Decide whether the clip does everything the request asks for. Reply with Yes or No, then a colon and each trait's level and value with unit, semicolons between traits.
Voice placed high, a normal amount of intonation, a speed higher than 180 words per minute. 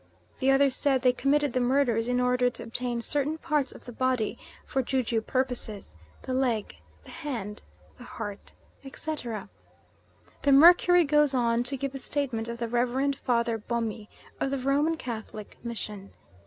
No: very high, 250 Hz; average, 3.0 semitones; average, 165 wpm